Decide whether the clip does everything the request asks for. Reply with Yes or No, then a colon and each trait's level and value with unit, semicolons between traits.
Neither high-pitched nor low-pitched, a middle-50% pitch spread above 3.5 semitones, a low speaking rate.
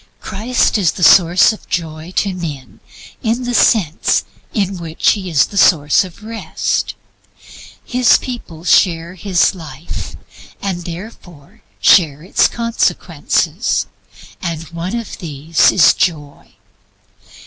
Yes: medium, 175 Hz; average, 4.1 semitones; slow, 120 wpm